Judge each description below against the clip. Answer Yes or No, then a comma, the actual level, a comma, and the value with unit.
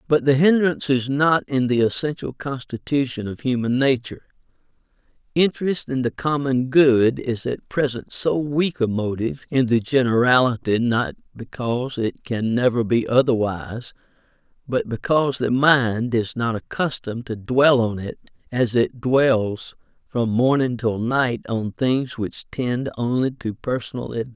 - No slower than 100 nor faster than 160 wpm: Yes, average, 150 wpm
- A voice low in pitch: Yes, low, 125 Hz